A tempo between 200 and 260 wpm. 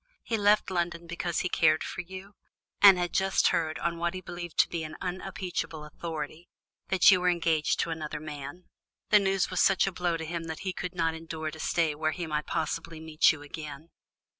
Yes: fast, 205 wpm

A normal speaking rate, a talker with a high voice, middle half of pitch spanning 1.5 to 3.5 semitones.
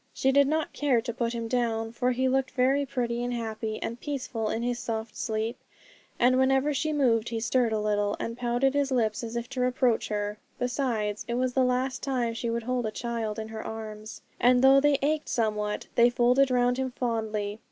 No: fast, 210 wpm; high, 240 Hz; narrow, 2.6 semitones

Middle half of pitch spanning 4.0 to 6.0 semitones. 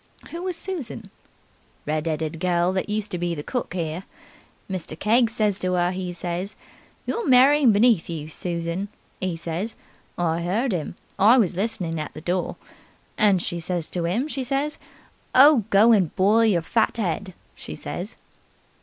Yes: average, 4.9 semitones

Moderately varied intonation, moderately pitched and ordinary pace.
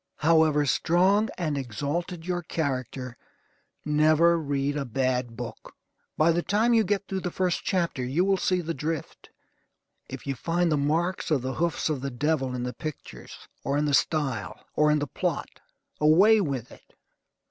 Yes: average, 4.2 semitones; medium, 155 Hz; average, 170 wpm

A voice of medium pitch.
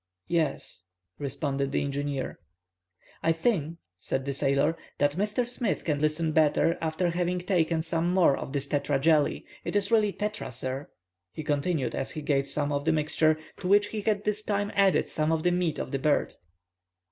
Yes: medium, 160 Hz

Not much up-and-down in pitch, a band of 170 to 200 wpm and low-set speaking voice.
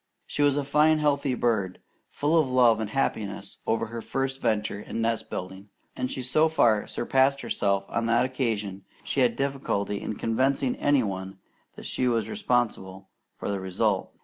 No: average, 4.8 semitones; average, 175 wpm; low, 120 Hz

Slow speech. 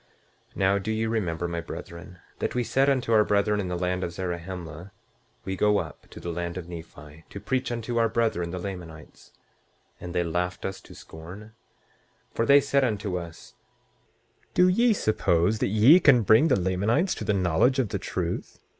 No: average, 190 wpm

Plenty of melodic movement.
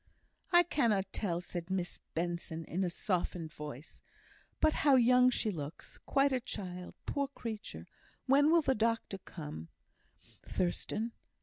Yes: wide, 6.8 semitones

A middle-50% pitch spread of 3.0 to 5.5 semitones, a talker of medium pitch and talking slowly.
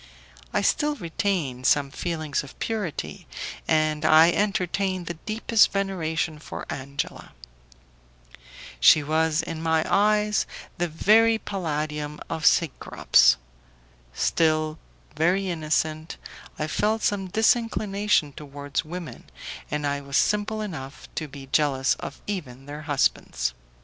Yes: average, 4.9 semitones; medium, 160 Hz; slow, 115 wpm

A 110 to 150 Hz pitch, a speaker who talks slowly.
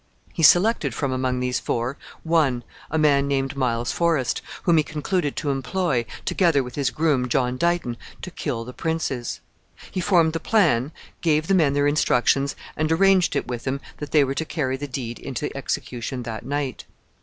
No: medium, 140 Hz; average, 180 wpm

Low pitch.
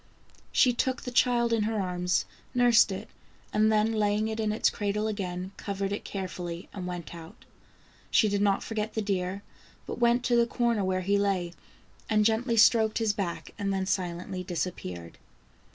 No: high, 205 Hz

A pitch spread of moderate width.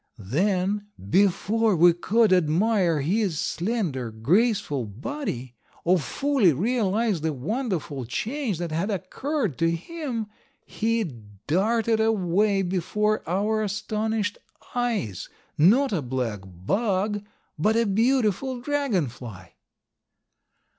No: wide, 5.9 semitones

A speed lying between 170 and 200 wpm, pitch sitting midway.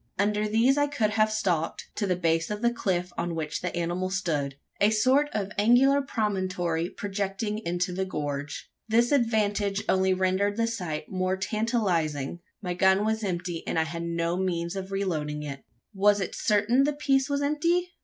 No: average, 175 wpm; high, 195 Hz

